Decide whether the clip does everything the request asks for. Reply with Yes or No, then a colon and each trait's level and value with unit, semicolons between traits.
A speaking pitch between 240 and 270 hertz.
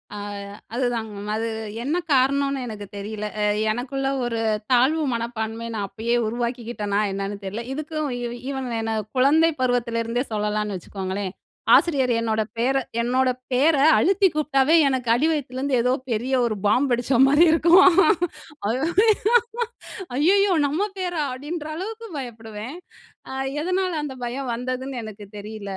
Yes: very high, 250 Hz